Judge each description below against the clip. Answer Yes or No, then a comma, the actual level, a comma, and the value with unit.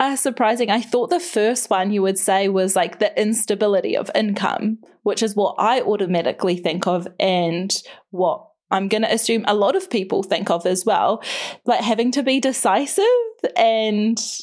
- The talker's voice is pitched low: No, high, 215 Hz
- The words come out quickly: No, average, 180 wpm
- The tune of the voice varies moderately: Yes, average, 4.0 semitones